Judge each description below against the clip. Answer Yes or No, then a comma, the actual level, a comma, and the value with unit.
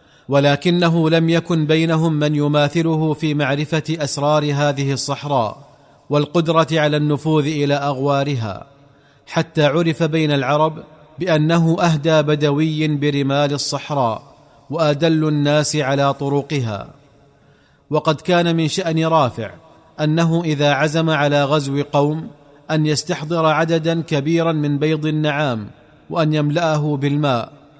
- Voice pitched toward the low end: No, medium, 150 Hz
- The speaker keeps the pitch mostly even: Yes, narrow, 2.0 semitones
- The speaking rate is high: No, average, 110 wpm